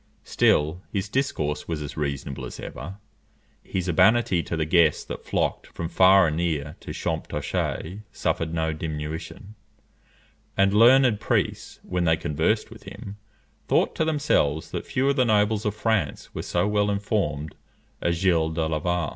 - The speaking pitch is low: Yes, very low, 85 Hz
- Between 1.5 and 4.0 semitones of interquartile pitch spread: No, average, 4.7 semitones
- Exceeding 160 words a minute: No, average, 155 wpm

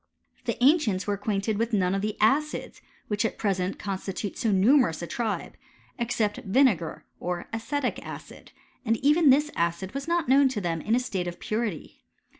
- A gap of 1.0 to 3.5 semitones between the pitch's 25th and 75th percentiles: No, average, 5.3 semitones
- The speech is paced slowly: No, average, 180 wpm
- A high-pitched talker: Yes, high, 215 Hz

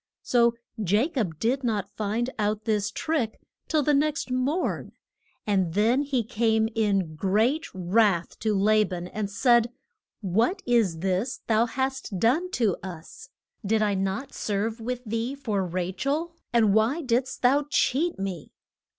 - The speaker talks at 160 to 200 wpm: No, average, 150 wpm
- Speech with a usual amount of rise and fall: Yes, average, 4.4 semitones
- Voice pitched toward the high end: Yes, high, 225 Hz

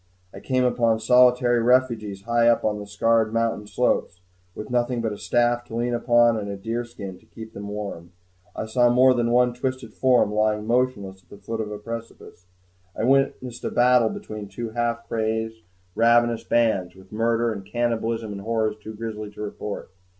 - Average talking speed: Yes, average, 185 wpm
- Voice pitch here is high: No, low, 115 Hz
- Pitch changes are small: Yes, narrow, 2.2 semitones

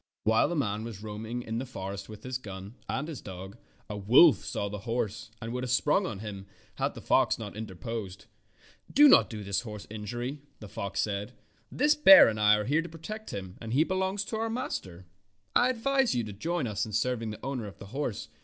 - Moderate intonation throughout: No, wide, 6.3 semitones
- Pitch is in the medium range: No, low, 115 Hz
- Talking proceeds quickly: Yes, fast, 215 wpm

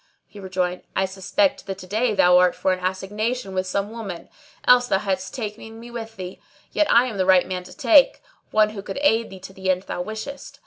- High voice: Yes, high, 200 Hz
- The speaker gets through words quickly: Yes, fast, 225 wpm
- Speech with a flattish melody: No, average, 3.4 semitones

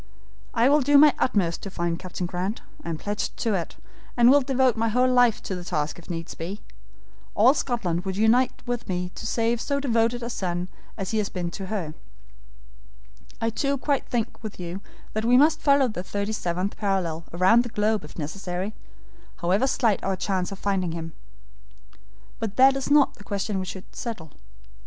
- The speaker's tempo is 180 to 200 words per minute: Yes, average, 195 wpm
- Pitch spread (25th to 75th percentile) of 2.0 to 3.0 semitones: No, average, 5.2 semitones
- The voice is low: No, high, 205 Hz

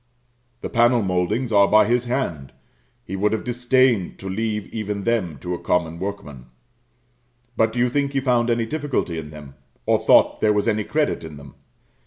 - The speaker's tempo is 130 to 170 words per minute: No, average, 185 wpm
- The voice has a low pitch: Yes, low, 105 Hz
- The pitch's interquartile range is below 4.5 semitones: No, average, 5.2 semitones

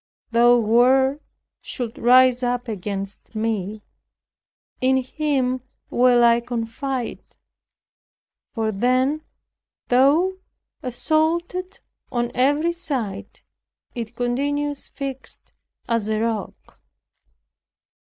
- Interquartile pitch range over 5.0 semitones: No, average, 3.2 semitones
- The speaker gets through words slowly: Yes, slow, 85 wpm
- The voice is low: No, very high, 250 Hz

